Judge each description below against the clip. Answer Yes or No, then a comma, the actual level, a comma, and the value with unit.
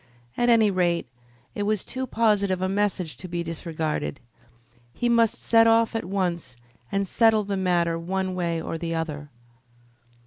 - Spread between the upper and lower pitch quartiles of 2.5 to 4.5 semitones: Yes, average, 4.2 semitones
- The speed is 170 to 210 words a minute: No, average, 160 wpm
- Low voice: No, medium, 185 Hz